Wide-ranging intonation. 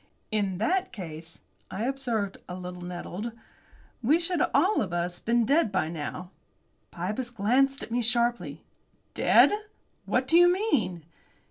Yes: wide, 7.1 semitones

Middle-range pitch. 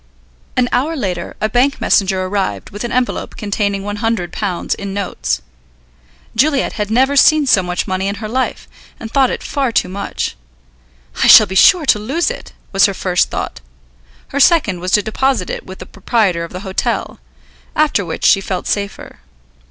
No: high, 205 Hz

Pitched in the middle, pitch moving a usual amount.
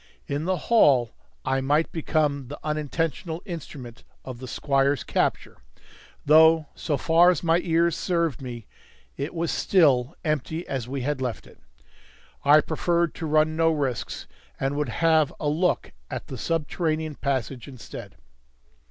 Yes: medium, 150 Hz; average, 3.3 semitones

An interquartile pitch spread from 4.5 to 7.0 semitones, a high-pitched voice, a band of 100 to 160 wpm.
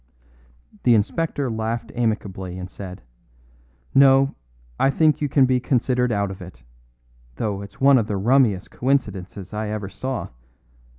No: average, 5.0 semitones; low, 110 Hz; average, 140 wpm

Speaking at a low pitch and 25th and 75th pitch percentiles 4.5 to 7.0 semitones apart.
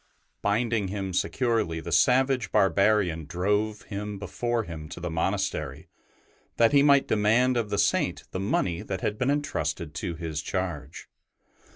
Yes: low, 100 Hz; average, 5.0 semitones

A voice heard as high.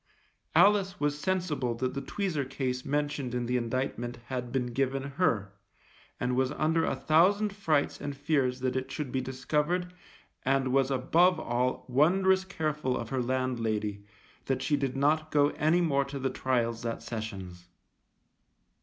No: low, 135 Hz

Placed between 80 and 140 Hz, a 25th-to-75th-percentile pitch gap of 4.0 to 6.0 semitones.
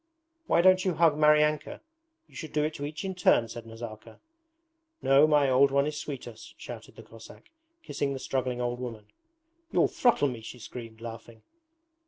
Yes: low, 135 Hz; average, 4.5 semitones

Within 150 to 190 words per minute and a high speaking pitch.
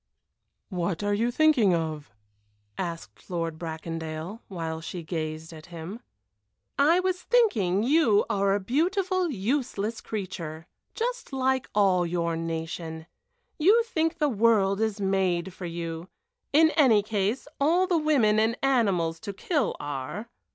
No: slow, 135 wpm; high, 200 Hz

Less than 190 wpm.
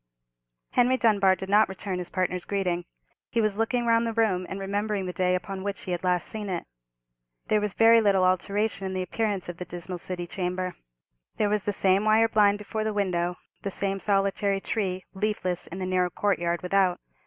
No: average, 200 wpm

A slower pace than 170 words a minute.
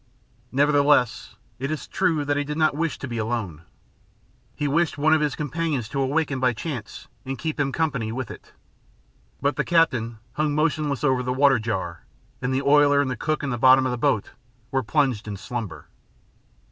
No: average, 190 wpm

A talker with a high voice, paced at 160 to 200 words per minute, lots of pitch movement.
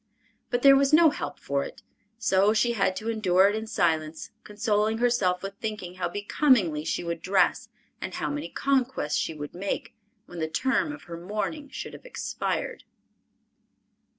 Yes: high, 205 Hz; average, 170 wpm; wide, 5.7 semitones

